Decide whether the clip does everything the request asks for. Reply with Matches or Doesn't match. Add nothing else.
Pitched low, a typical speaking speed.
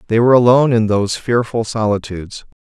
Matches